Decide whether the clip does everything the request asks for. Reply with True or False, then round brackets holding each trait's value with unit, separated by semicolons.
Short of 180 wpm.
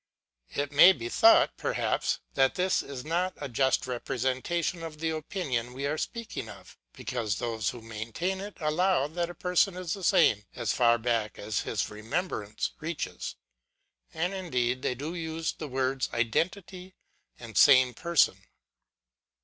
True (155 wpm)